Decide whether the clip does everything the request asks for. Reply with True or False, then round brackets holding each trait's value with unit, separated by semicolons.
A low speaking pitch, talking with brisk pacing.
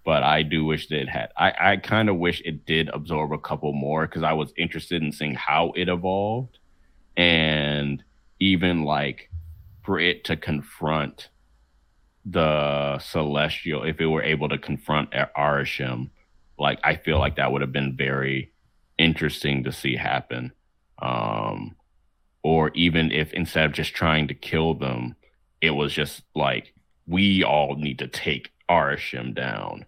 False (75 Hz; 160 wpm)